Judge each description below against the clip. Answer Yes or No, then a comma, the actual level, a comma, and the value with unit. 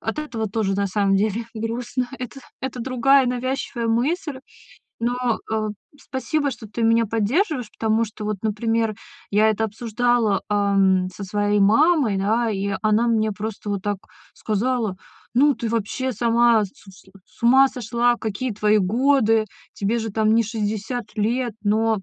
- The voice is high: Yes, high, 225 Hz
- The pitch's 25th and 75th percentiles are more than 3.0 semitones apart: No, average, 2.7 semitones